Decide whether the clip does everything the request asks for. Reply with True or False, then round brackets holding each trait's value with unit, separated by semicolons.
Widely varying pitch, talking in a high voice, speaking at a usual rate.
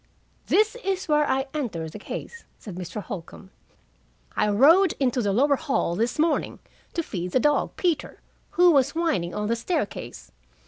True (7.9 semitones; 265 Hz; 165 wpm)